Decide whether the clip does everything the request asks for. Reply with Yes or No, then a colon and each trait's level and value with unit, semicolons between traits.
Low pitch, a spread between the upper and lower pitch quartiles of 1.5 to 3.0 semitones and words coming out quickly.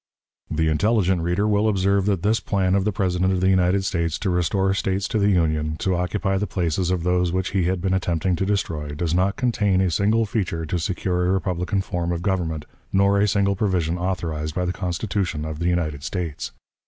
Yes: very low, 90 Hz; narrow, 2.5 semitones; fast, 210 wpm